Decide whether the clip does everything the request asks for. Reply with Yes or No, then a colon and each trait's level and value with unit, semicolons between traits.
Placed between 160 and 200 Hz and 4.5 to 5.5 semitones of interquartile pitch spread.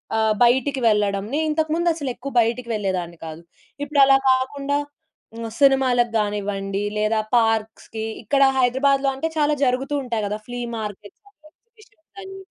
No: very high, 250 Hz; average, 5.1 semitones